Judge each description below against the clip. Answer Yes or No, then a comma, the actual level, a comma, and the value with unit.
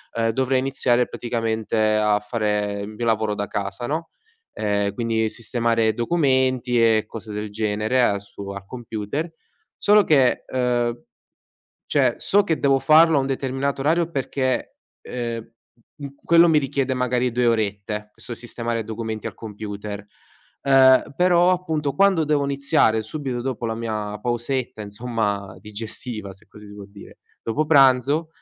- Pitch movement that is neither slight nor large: Yes, average, 4.1 semitones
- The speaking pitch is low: Yes, low, 120 Hz